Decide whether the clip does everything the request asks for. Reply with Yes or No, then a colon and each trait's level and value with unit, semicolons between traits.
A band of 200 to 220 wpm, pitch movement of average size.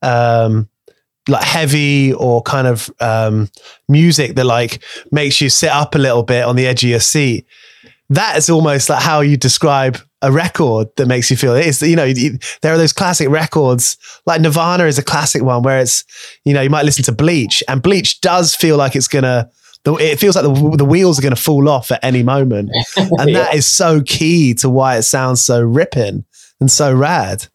Yes: fast, 205 wpm; average, 3.7 semitones